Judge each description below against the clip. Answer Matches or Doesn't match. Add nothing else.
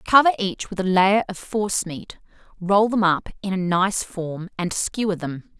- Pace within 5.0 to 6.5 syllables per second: Doesn't match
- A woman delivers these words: Matches